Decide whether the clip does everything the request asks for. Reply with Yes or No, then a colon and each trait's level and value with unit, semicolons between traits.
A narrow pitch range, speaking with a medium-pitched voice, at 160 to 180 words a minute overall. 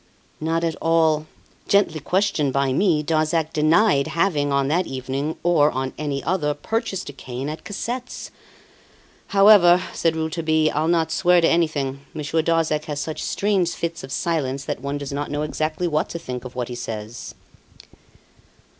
No: average, 3.1 semitones; medium, 155 Hz; average, 165 wpm